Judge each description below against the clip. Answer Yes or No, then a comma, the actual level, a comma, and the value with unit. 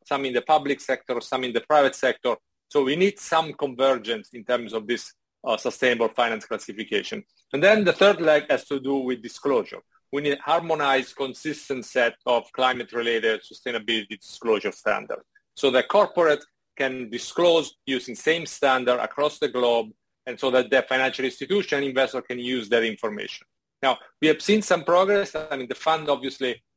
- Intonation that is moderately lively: Yes, average, 4.0 semitones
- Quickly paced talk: No, average, 175 wpm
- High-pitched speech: No, low, 135 Hz